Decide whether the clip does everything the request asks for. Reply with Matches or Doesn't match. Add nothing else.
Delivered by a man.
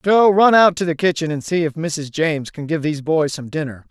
Matches